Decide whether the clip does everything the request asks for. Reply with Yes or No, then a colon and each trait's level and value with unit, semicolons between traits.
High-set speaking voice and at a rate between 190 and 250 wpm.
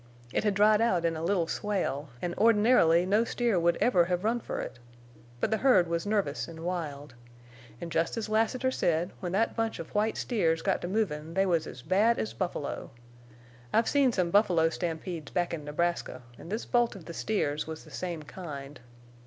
No: medium, 175 Hz; average, 195 wpm